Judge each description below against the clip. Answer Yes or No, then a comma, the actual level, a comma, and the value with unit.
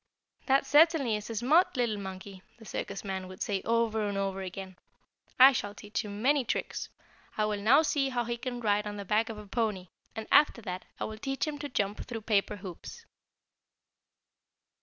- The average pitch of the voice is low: No, high, 215 Hz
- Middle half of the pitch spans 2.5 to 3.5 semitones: No, average, 3.9 semitones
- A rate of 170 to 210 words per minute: Yes, average, 195 wpm